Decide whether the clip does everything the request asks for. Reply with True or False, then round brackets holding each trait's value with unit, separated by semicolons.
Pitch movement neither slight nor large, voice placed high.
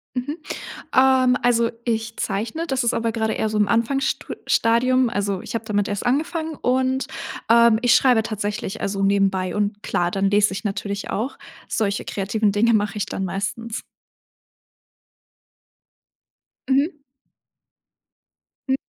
True (3.6 semitones; 225 Hz)